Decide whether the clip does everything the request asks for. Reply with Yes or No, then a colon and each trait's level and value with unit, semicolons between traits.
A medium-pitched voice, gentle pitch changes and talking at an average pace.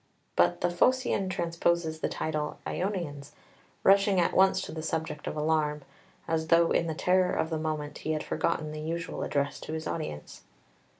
Yes: medium, 160 Hz; narrow, 2.3 semitones; average, 175 wpm